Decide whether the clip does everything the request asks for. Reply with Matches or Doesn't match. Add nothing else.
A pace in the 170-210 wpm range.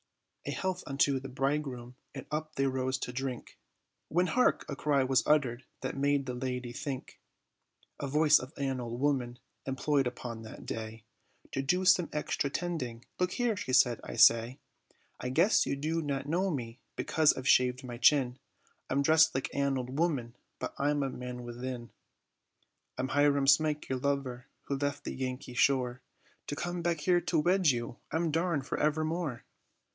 Matches